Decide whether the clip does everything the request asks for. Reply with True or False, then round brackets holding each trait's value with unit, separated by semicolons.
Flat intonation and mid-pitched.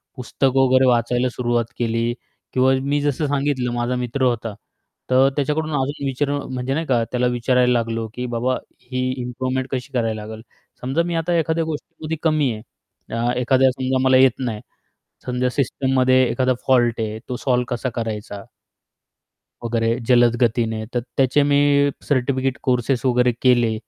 False (2.0 semitones; 125 Hz)